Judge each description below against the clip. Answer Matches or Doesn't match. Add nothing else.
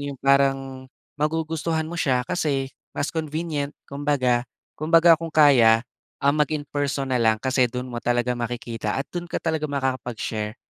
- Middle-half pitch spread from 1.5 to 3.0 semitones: Doesn't match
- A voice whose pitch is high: Doesn't match